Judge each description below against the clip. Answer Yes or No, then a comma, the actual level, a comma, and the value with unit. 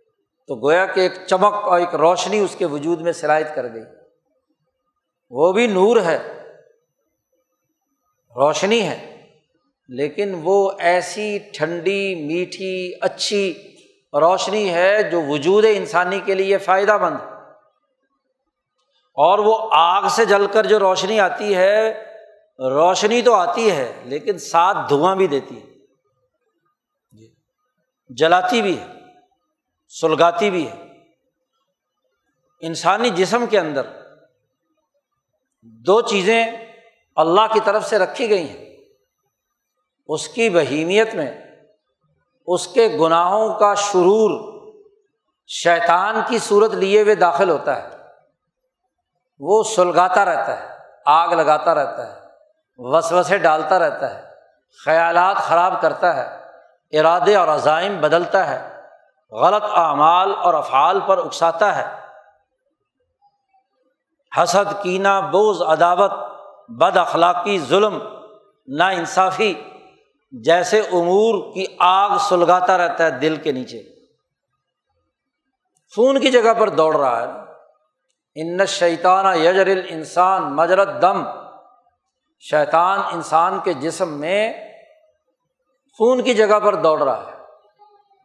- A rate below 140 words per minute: Yes, average, 115 wpm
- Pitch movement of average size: No, wide, 5.9 semitones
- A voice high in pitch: Yes, high, 200 Hz